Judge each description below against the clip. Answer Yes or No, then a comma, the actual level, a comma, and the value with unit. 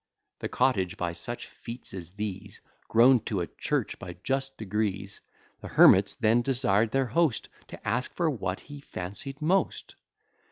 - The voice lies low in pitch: Yes, low, 110 Hz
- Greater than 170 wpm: No, average, 155 wpm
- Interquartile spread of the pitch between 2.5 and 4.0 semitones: No, wide, 5.6 semitones